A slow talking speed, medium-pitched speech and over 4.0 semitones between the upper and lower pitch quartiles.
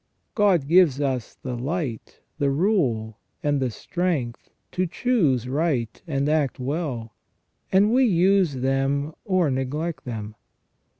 Yes: slow, 125 wpm; medium, 145 Hz; wide, 5.6 semitones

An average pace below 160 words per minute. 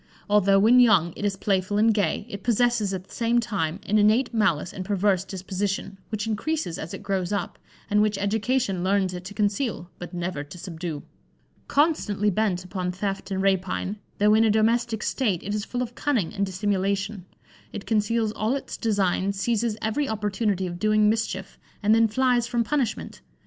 No: average, 180 wpm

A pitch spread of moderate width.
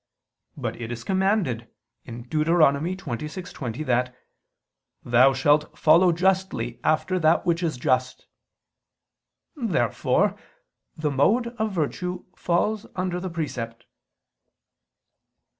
No: wide, 6.4 semitones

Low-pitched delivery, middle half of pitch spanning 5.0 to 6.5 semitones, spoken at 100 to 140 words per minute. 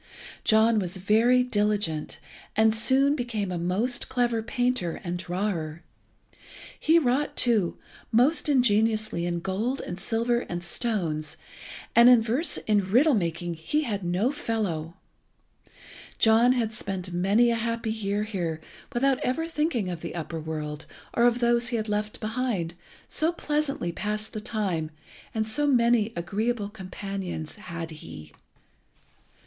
No: high, 215 Hz; wide, 5.4 semitones; slow, 135 wpm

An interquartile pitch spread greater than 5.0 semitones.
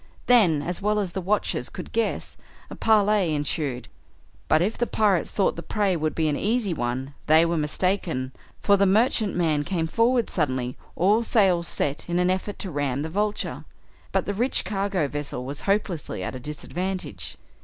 Yes: wide, 5.6 semitones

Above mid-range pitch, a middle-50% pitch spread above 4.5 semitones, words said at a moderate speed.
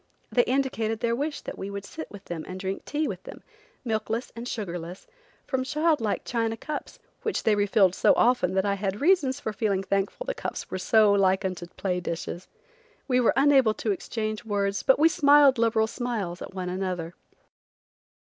Yes: high, 220 Hz; average, 5.2 semitones; average, 190 wpm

